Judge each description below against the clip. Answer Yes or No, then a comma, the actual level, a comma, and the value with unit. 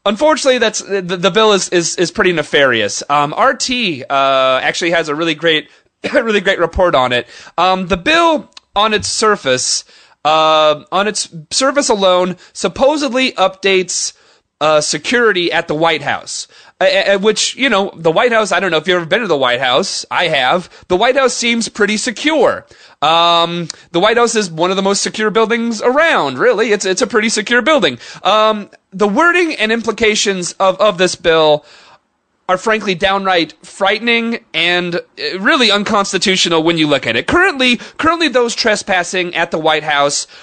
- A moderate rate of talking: Yes, average, 170 wpm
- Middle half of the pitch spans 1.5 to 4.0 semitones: No, average, 5.2 semitones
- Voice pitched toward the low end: No, high, 195 Hz